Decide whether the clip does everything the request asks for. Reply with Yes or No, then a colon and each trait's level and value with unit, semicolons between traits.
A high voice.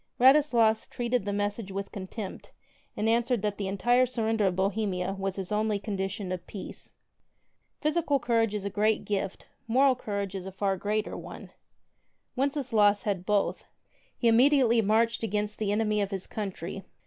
Yes: high, 210 Hz